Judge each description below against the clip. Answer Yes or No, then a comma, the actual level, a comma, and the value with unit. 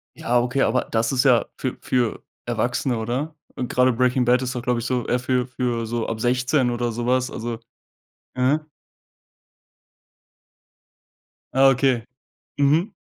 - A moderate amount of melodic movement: No, narrow, 1.4 semitones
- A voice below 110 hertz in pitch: No, low, 125 Hz